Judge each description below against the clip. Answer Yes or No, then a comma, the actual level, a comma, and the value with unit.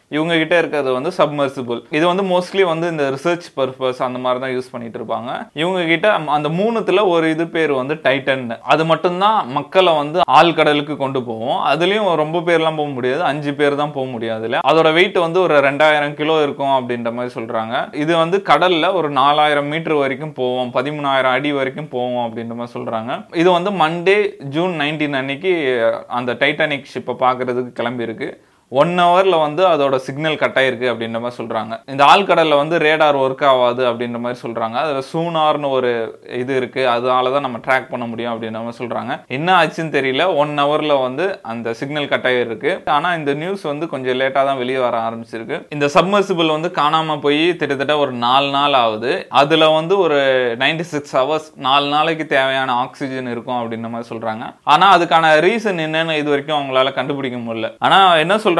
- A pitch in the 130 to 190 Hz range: Yes, medium, 140 Hz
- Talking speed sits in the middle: No, fast, 175 wpm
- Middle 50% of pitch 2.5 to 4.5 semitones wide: Yes, average, 4.0 semitones